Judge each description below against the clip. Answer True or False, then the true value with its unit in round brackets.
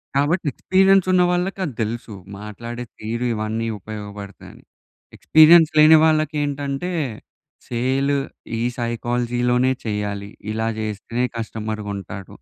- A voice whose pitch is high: False (120 Hz)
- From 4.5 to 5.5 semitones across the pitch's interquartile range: True (5.2 semitones)